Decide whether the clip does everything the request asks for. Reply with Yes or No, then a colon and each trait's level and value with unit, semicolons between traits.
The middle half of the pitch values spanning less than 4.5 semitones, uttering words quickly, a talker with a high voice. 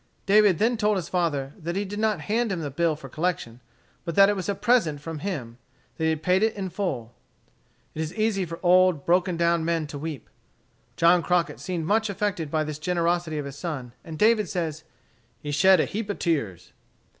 No: average, 4.1 semitones; fast, 215 wpm; medium, 170 Hz